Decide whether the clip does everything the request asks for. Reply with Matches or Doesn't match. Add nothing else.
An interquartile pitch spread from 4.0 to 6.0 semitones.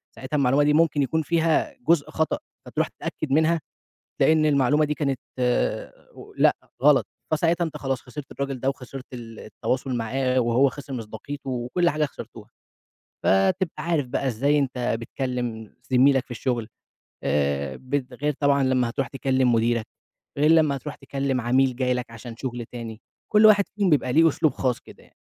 Doesn't match